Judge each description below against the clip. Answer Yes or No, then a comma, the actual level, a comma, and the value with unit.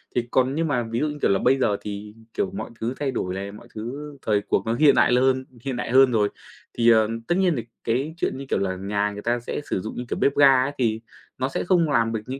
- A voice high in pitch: No, low, 120 Hz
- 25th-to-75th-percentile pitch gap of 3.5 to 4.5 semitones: Yes, average, 4.0 semitones